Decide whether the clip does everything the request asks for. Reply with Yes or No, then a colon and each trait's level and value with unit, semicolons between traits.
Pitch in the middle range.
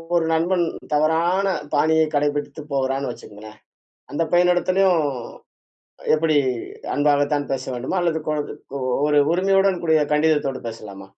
Yes: medium, 155 Hz